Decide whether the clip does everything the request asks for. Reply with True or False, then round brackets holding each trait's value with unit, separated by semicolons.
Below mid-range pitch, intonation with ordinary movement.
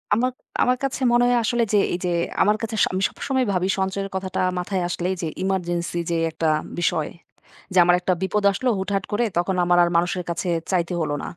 False (190 Hz; 3.1 semitones)